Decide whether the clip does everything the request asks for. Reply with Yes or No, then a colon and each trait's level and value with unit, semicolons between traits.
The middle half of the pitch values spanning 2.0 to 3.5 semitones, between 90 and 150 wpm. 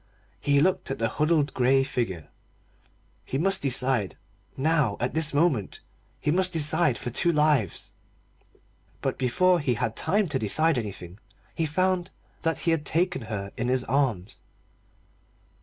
No: wide, 5.4 semitones; average, 145 wpm